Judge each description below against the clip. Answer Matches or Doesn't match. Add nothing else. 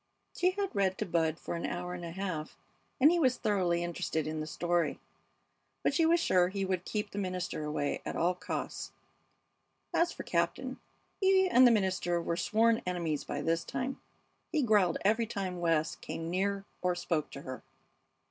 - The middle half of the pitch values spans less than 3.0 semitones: Doesn't match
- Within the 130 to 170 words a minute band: Doesn't match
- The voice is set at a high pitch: Doesn't match